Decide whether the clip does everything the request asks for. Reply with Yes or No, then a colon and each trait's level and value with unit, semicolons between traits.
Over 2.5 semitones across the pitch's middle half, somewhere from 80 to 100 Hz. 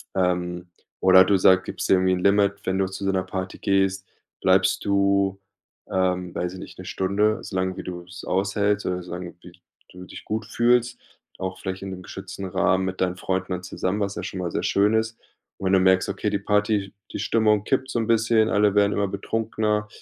No: narrow, 1.8 semitones; very low, 95 Hz